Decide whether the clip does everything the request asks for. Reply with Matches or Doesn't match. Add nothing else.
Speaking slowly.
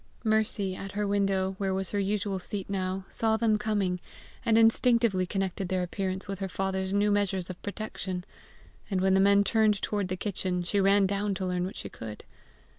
Doesn't match